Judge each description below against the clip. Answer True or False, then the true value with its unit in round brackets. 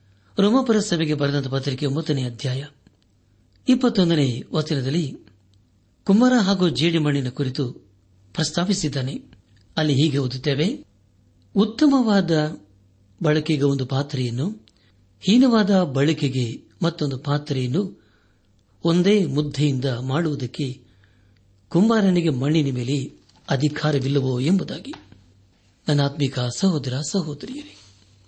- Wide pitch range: True (7.7 semitones)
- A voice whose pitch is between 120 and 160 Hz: True (140 Hz)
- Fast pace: False (75 wpm)